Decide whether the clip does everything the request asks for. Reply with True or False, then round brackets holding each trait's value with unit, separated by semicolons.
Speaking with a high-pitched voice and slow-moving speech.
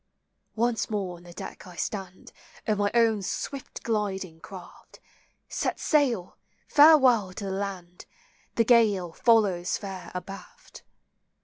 True (200 Hz; 125 wpm)